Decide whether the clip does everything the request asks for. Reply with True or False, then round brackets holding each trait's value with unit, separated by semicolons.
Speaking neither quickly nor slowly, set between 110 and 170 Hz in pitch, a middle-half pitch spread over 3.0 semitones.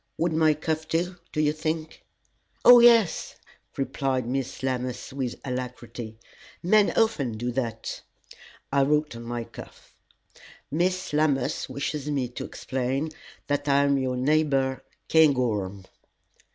False (125 wpm; 140 Hz; 3.7 semitones)